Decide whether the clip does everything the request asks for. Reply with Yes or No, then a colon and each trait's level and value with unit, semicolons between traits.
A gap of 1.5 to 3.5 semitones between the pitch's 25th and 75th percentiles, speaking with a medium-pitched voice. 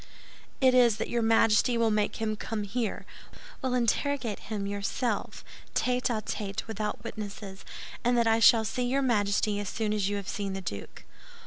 No: average, 2.7 semitones; high, 220 Hz